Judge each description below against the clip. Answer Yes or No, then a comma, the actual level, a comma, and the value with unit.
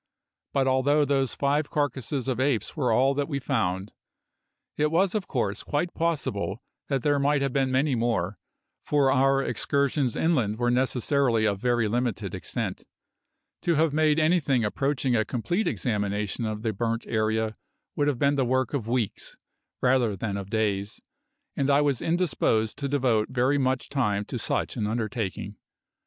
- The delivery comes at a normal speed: Yes, average, 165 wpm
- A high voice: No, low, 130 Hz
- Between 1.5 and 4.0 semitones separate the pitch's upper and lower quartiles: No, average, 4.4 semitones